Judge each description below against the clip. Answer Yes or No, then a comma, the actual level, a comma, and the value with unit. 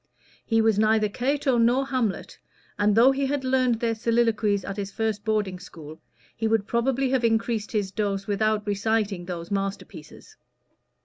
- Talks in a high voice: Yes, high, 220 Hz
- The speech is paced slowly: No, average, 165 wpm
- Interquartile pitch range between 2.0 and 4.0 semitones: Yes, average, 2.8 semitones